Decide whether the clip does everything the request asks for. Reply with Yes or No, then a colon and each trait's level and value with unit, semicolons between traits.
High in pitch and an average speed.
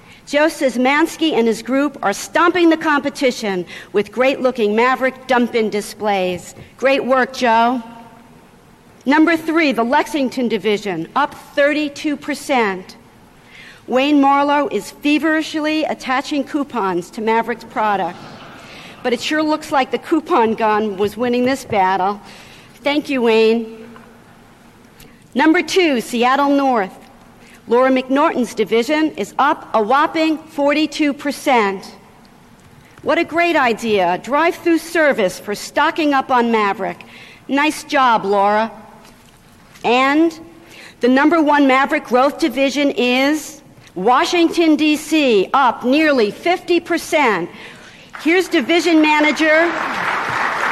No: very high, 270 Hz; slow, 110 wpm